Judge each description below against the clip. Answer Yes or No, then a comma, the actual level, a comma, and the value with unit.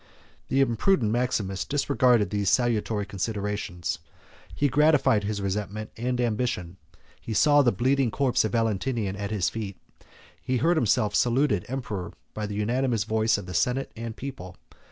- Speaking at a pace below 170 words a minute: Yes, average, 155 wpm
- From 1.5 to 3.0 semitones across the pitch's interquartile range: No, average, 3.8 semitones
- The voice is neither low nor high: No, low, 110 Hz